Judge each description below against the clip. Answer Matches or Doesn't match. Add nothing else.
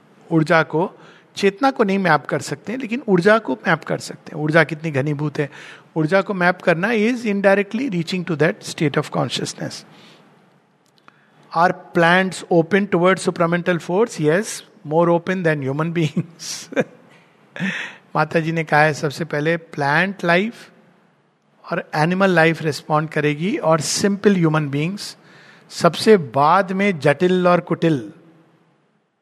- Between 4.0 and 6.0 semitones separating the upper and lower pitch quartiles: Doesn't match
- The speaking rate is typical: Matches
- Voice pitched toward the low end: Doesn't match